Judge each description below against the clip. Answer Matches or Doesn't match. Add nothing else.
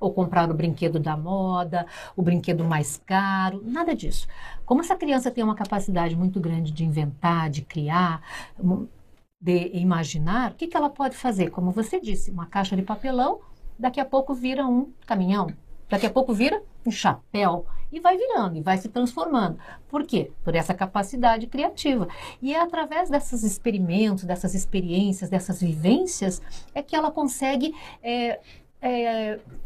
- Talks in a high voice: Matches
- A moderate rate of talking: Matches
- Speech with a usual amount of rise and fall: Doesn't match